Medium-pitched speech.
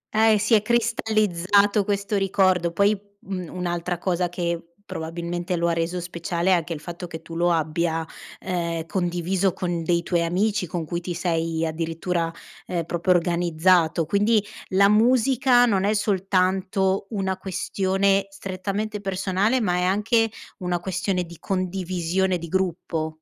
Yes: medium, 180 Hz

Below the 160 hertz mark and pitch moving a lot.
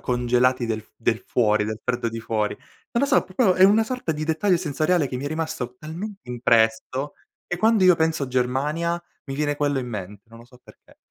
Yes: low, 135 Hz; wide, 6.0 semitones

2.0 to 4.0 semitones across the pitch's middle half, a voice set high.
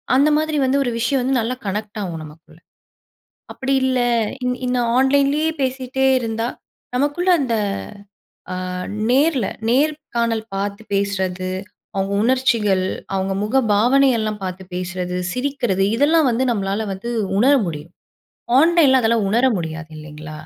No: wide, 5.5 semitones; high, 235 Hz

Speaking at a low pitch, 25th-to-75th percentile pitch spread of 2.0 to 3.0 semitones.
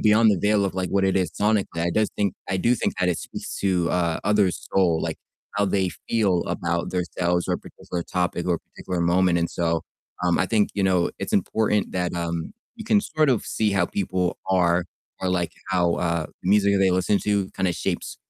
Yes: very low, 95 Hz; narrow, 2.6 semitones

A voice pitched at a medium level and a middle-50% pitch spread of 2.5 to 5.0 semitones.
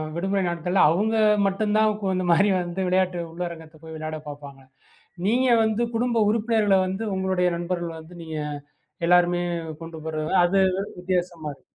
Yes: medium, 180 Hz; average, 3.1 semitones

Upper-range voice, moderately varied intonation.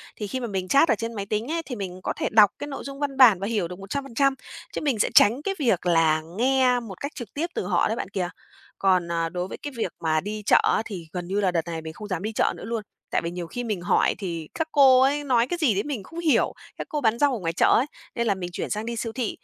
No: high, 215 Hz; wide, 6.3 semitones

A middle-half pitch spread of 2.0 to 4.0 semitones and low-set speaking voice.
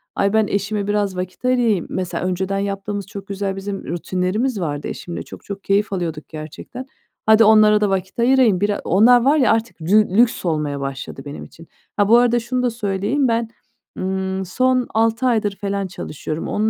No: average, 3.4 semitones; high, 200 Hz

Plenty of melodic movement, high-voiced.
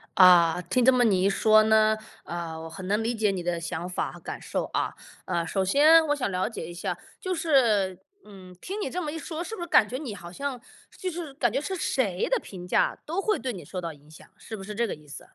Yes: wide, 7.8 semitones; high, 215 Hz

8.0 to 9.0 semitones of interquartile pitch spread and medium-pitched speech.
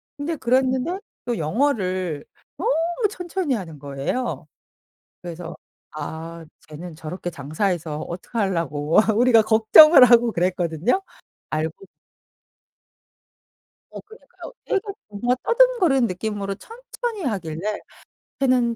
No: wide, 8.3 semitones; high, 215 Hz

